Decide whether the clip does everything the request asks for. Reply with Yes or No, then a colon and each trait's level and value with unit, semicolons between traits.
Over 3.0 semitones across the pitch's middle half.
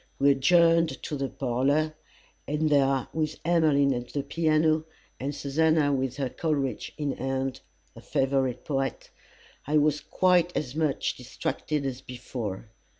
No: average, 2.7 semitones